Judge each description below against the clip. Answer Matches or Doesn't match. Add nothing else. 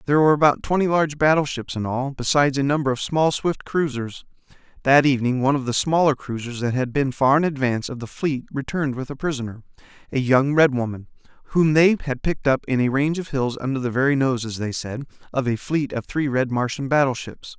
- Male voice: Matches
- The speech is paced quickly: Matches